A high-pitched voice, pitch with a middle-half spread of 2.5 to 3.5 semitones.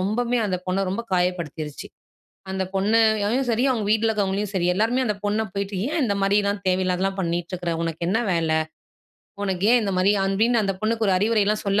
Yes: high, 200 Hz; average, 3.0 semitones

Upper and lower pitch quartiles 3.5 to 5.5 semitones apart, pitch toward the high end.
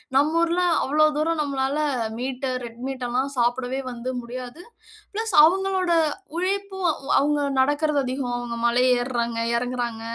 Yes: average, 4.6 semitones; very high, 270 Hz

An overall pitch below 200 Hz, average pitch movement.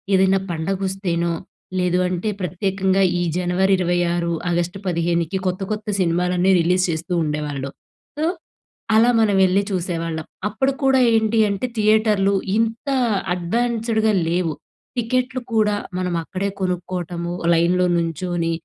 Yes: medium, 185 Hz; average, 3.4 semitones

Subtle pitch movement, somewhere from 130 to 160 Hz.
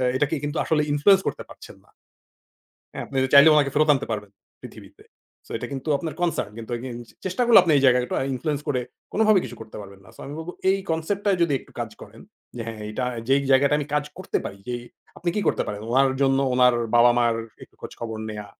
No: average, 5.0 semitones; low, 135 Hz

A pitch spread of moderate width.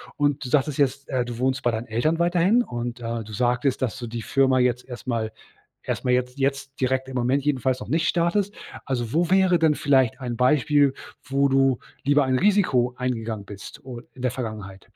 Yes: average, 3.0 semitones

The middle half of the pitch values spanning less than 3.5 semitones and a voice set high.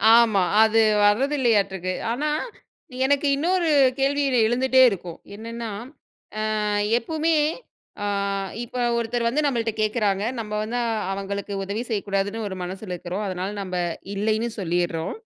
No: average, 3.8 semitones; high, 220 Hz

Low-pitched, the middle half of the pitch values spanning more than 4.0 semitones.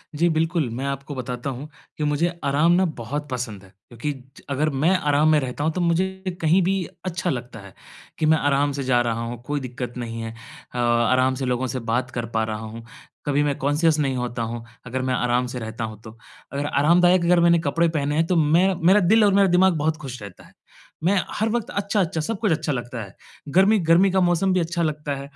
No: medium, 145 Hz; wide, 5.5 semitones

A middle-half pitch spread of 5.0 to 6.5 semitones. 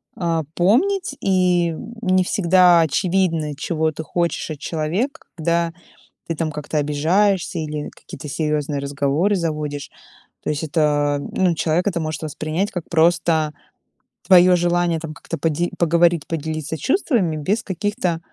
No: average, 2.9 semitones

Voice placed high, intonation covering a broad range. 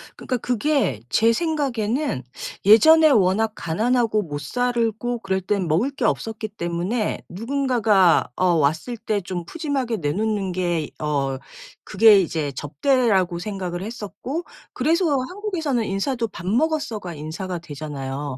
Yes: high, 215 Hz; wide, 6.3 semitones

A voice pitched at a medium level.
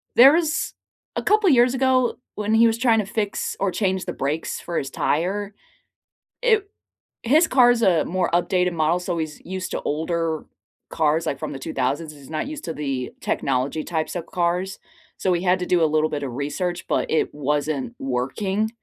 Yes: medium, 175 Hz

